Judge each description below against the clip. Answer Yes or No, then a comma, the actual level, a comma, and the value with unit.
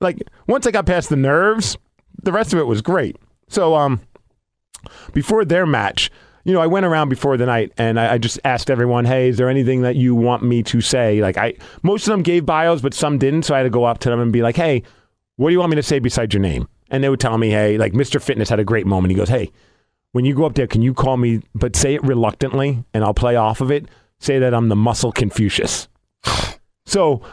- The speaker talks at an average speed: No, fast, 255 wpm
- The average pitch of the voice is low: Yes, low, 125 Hz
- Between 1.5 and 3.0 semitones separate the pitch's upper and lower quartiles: No, average, 4.1 semitones